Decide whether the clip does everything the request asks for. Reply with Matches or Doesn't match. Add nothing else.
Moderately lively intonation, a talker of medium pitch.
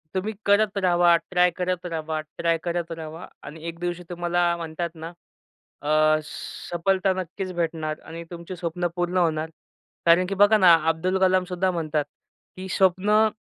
Doesn't match